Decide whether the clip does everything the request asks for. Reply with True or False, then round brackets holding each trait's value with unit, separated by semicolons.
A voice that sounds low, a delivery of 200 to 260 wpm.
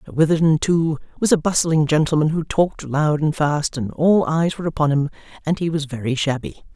False (155 Hz; 205 wpm)